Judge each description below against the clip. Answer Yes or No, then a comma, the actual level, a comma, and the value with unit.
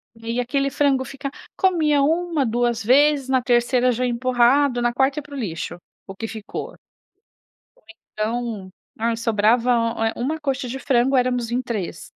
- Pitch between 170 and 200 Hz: No, very high, 250 Hz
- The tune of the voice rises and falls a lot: No, average, 2.9 semitones